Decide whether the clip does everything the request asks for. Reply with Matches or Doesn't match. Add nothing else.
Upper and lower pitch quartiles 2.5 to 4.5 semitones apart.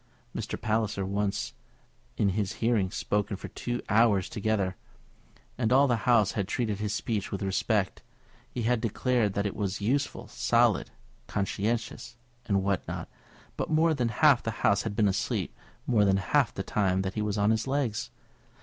Matches